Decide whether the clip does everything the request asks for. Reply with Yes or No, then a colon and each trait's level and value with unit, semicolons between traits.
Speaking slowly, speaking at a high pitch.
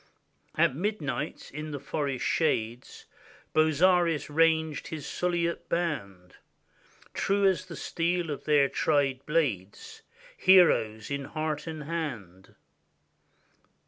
No: slow, 105 wpm; medium, 155 Hz